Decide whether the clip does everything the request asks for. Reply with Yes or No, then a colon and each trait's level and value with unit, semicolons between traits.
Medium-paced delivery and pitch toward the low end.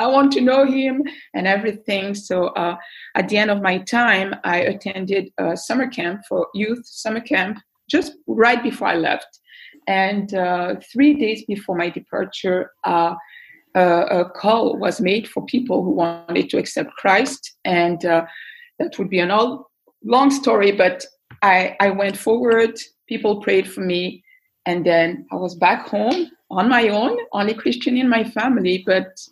No: average, 170 wpm; high, 210 Hz